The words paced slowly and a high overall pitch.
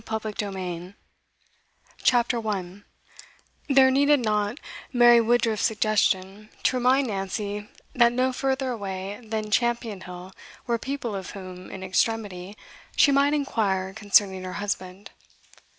Yes: slow, 130 wpm; high, 215 Hz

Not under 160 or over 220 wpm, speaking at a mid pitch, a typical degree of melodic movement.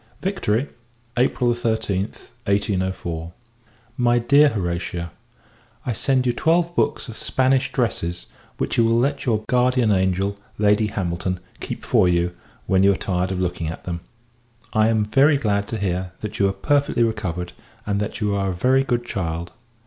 No: average, 165 wpm; low, 105 Hz; average, 4.8 semitones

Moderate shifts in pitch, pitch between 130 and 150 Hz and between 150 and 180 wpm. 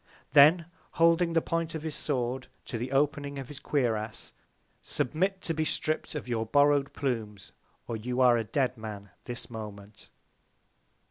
Yes: average, 5.0 semitones; low, 135 Hz; average, 155 wpm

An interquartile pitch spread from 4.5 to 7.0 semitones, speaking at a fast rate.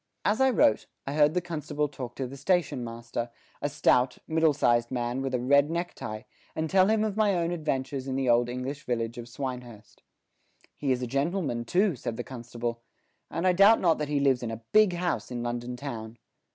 Yes: wide, 5.4 semitones; fast, 210 wpm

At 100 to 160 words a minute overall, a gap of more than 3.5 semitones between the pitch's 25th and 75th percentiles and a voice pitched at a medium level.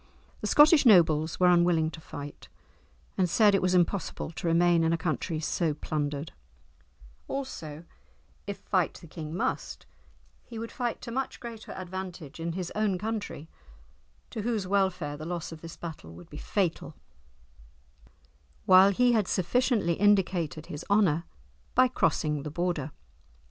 Yes: average, 150 wpm; average, 4.2 semitones; medium, 175 Hz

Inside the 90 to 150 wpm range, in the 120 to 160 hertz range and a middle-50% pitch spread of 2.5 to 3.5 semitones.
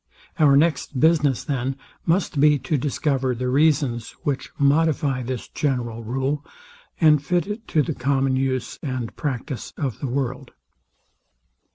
Yes: average, 140 wpm; medium, 140 Hz; average, 2.8 semitones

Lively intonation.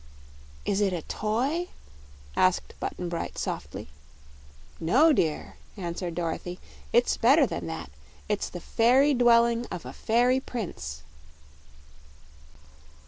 Yes: wide, 6.3 semitones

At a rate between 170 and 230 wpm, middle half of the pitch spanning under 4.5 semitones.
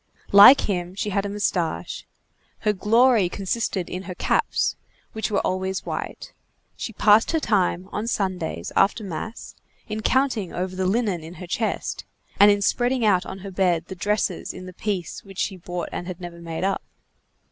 Yes: average, 180 wpm; average, 2.8 semitones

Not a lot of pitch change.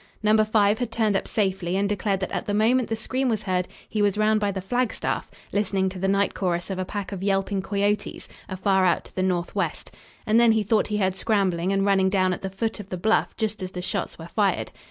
Yes: narrow, 2.3 semitones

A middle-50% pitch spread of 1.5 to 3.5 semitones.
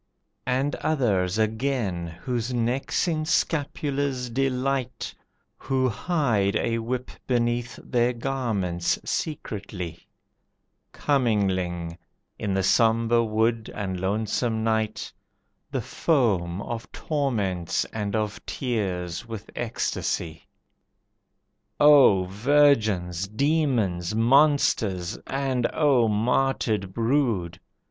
No: average, 5.3 semitones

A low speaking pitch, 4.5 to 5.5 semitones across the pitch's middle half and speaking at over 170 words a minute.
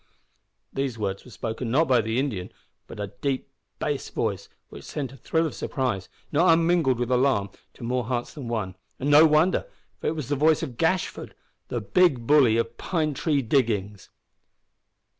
Yes: low, 130 Hz; average, 4.9 semitones; average, 180 wpm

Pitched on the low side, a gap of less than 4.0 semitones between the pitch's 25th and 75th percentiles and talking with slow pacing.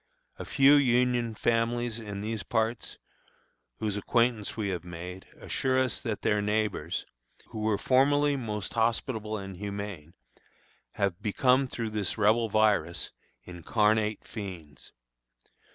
Yes: low, 110 Hz; average, 3.0 semitones; slow, 120 wpm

